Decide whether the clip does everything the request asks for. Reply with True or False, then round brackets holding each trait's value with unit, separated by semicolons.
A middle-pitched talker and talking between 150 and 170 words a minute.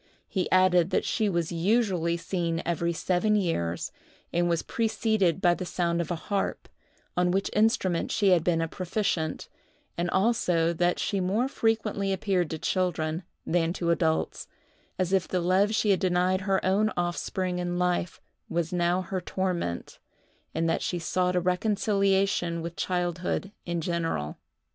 True (180 Hz; 155 wpm)